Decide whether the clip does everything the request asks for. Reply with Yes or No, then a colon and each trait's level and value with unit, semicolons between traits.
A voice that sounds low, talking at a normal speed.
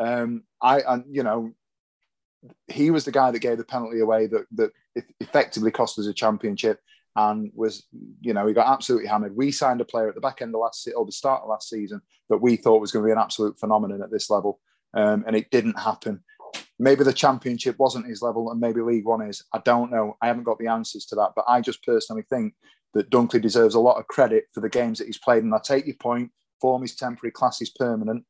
No: low, 115 Hz; fast, 240 wpm